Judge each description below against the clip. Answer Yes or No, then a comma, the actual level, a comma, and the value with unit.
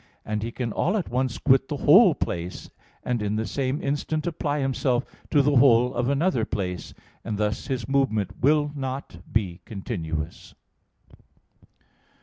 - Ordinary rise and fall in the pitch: Yes, average, 5.0 semitones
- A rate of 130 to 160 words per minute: Yes, average, 150 wpm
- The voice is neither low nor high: No, low, 130 Hz